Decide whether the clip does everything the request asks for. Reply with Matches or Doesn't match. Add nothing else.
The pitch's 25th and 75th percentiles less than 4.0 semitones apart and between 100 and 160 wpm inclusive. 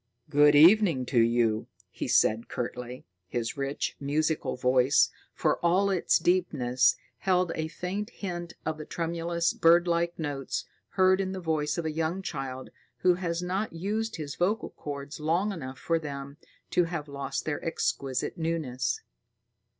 Doesn't match